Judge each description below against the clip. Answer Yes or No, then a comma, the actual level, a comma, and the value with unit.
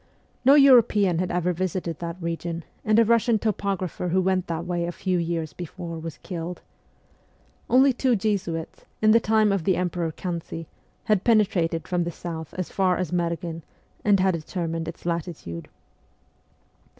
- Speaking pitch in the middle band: Yes, medium, 180 Hz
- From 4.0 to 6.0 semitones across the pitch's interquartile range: No, average, 3.1 semitones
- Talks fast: No, average, 160 wpm